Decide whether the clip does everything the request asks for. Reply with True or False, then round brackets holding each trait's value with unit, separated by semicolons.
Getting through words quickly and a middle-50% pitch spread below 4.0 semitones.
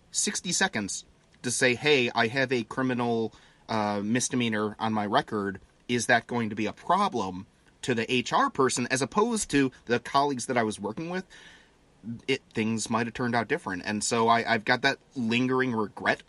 False (185 wpm; 3.0 semitones)